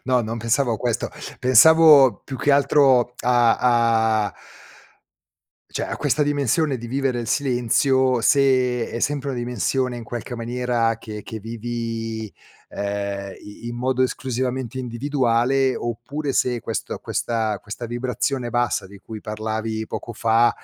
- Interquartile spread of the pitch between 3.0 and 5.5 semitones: No, narrow, 2.6 semitones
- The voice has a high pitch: No, low, 120 Hz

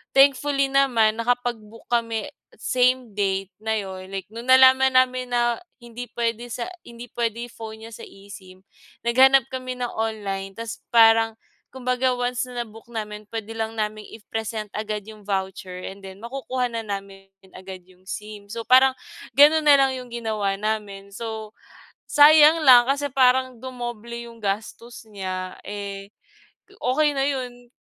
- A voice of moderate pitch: No, high, 230 Hz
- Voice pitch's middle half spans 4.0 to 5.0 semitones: No, average, 3.3 semitones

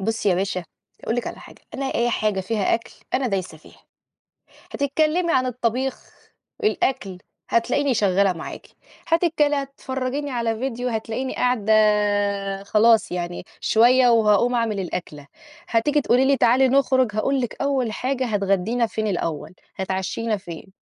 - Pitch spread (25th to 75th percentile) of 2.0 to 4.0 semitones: No, average, 4.6 semitones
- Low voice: No, high, 230 Hz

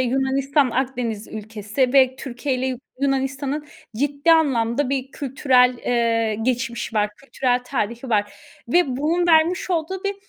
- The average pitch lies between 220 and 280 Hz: Yes, very high, 260 Hz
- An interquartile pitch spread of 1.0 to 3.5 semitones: Yes, average, 3.0 semitones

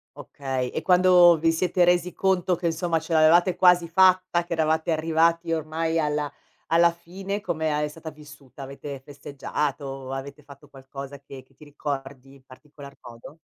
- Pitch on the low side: No, medium, 155 Hz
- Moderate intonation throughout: Yes, average, 3.6 semitones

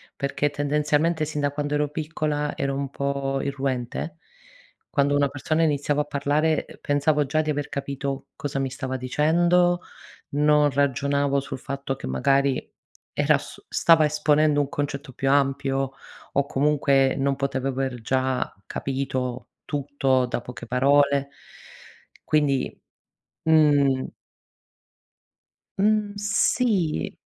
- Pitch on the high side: No, medium, 140 Hz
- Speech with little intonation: Yes, narrow, 1.7 semitones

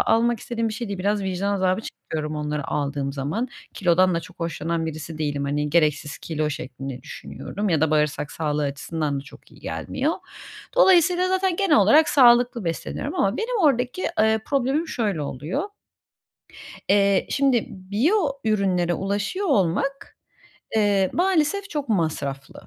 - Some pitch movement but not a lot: No, wide, 8.4 semitones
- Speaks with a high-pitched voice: Yes, high, 195 Hz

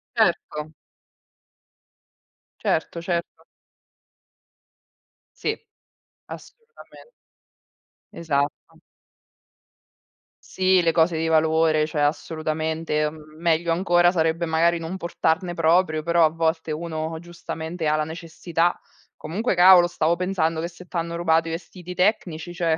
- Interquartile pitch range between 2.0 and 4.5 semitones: No, narrow, 1.5 semitones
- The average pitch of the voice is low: No, medium, 165 Hz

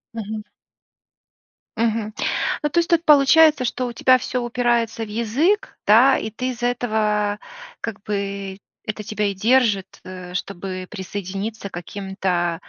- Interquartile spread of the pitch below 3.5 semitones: No, average, 3.8 semitones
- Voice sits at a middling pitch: No, high, 215 Hz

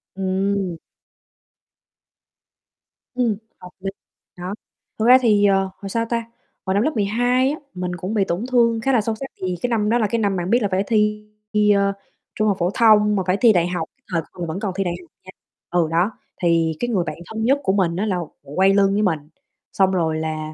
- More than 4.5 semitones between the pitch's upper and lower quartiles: No, average, 3.5 semitones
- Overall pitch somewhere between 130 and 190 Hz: No, high, 200 Hz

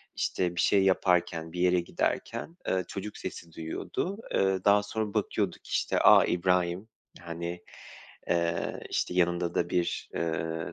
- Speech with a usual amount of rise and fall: No, narrow, 2.0 semitones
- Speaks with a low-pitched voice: Yes, very low, 90 Hz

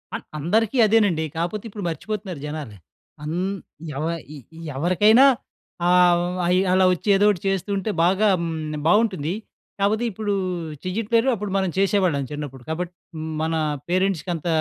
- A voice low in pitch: No, medium, 185 Hz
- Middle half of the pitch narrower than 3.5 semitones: No, average, 4.0 semitones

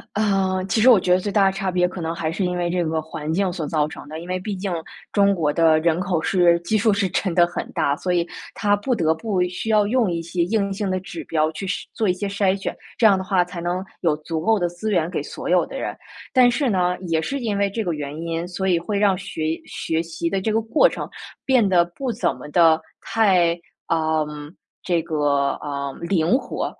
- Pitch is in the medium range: Yes, medium, 180 Hz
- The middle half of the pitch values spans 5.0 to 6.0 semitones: No, average, 3.4 semitones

